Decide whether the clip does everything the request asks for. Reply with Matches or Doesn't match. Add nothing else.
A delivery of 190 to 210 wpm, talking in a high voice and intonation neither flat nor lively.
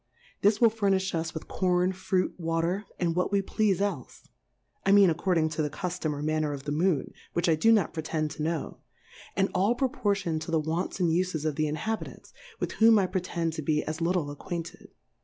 Doesn't match